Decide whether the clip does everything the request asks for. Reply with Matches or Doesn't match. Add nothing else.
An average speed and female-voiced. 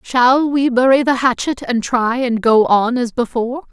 Matches